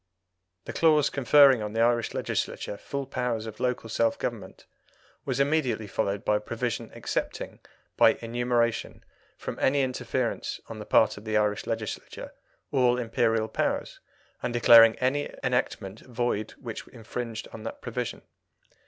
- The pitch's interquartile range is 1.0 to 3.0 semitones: Yes, narrow, 2.5 semitones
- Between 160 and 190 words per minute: No, average, 145 wpm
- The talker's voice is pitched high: No, low, 115 Hz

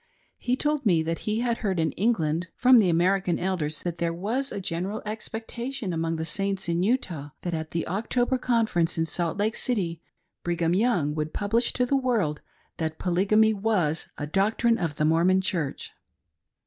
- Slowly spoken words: No, average, 175 wpm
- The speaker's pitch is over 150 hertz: Yes, medium, 185 Hz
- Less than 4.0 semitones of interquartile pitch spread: No, average, 5.2 semitones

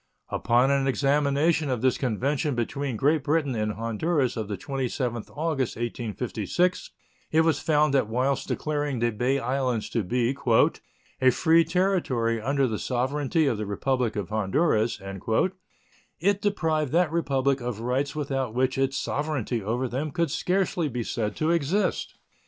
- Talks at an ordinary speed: Yes, average, 150 wpm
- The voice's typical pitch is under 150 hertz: Yes, low, 135 Hz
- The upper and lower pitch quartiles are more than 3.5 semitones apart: Yes, average, 4.3 semitones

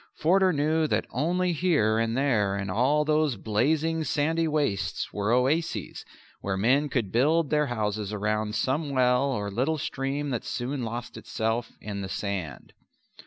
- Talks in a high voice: No, low, 125 Hz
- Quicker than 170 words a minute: No, average, 155 wpm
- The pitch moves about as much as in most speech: No, wide, 6.0 semitones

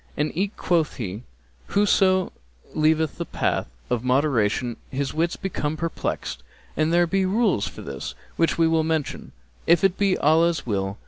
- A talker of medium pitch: Yes, medium, 160 Hz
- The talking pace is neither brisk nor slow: Yes, average, 155 wpm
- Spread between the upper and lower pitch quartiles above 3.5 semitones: Yes, wide, 5.6 semitones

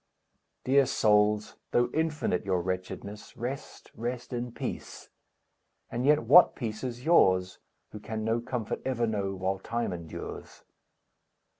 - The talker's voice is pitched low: Yes, low, 115 Hz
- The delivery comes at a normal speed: No, slow, 130 wpm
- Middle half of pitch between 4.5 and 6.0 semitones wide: No, average, 4.1 semitones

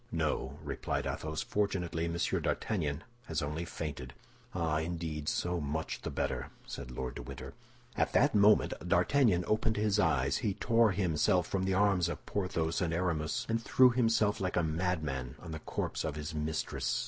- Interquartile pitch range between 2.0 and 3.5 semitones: No, average, 4.5 semitones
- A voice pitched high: No, very low, 85 Hz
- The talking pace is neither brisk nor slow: Yes, average, 170 wpm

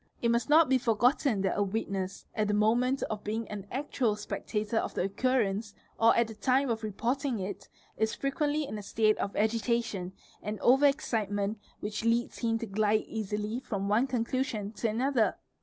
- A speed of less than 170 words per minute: No, average, 190 wpm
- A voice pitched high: Yes, high, 220 Hz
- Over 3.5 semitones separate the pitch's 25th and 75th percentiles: No, average, 3.1 semitones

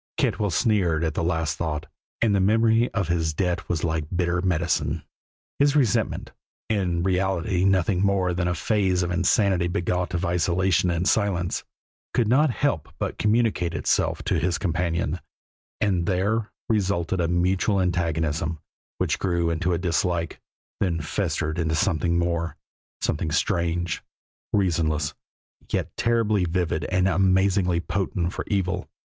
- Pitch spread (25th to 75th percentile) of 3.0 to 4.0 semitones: No, narrow, 2.4 semitones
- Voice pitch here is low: Yes, very low, 90 Hz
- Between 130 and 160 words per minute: Yes, average, 140 wpm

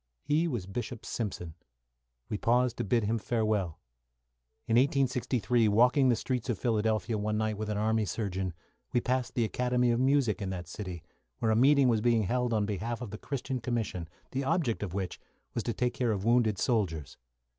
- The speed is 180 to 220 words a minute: Yes, average, 190 wpm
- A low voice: Yes, low, 115 Hz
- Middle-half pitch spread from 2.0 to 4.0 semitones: Yes, average, 3.1 semitones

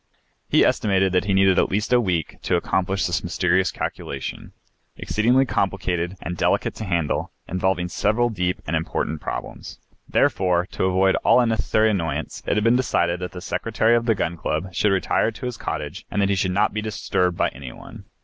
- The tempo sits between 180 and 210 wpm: Yes, average, 190 wpm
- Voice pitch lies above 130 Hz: No, very low, 95 Hz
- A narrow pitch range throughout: No, average, 3.3 semitones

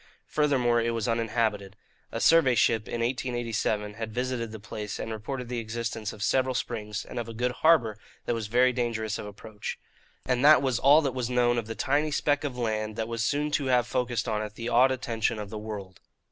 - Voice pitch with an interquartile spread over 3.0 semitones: No, narrow, 2.6 semitones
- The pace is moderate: No, fast, 215 wpm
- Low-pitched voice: Yes, low, 115 Hz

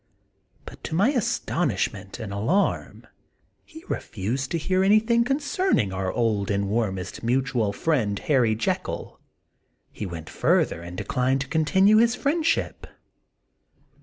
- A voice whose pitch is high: No, low, 130 Hz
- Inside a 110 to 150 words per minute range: Yes, slow, 135 wpm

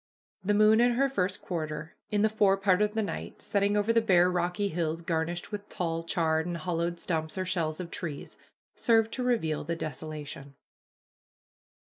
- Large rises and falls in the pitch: No, average, 4.3 semitones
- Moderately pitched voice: Yes, medium, 180 Hz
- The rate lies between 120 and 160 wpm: No, average, 175 wpm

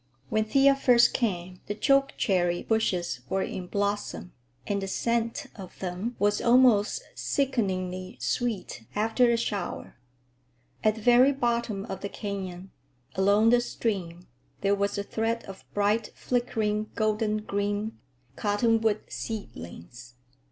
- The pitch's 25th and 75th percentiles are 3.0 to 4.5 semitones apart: Yes, average, 3.3 semitones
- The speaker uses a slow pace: Yes, slow, 125 wpm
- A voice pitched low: No, high, 210 Hz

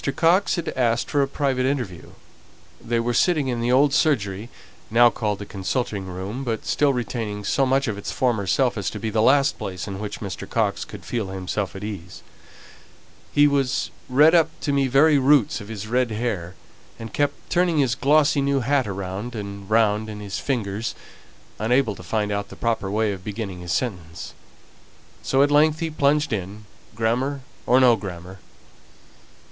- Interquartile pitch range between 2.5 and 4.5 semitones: No, average, 5.2 semitones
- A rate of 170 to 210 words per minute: Yes, average, 180 wpm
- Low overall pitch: Yes, low, 115 Hz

